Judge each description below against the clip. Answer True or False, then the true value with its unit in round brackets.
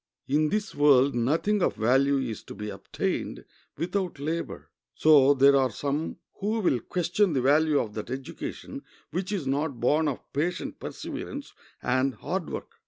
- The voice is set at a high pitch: False (145 Hz)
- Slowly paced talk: False (160 wpm)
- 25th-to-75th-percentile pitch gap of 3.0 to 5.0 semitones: True (4.1 semitones)